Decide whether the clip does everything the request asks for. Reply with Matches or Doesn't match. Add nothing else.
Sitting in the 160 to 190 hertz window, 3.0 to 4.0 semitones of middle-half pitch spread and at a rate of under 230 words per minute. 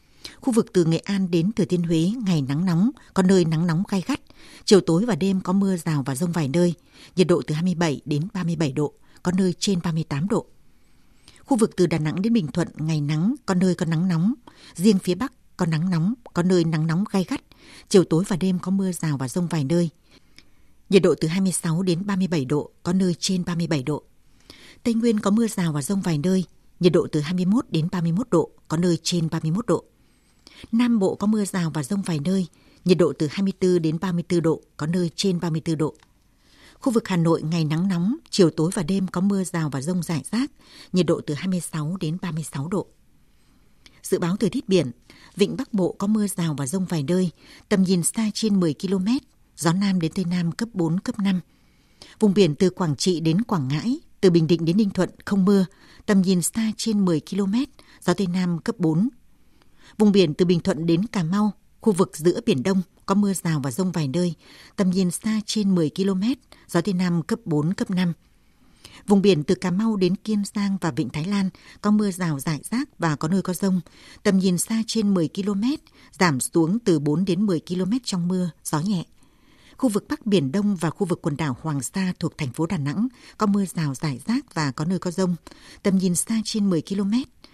Matches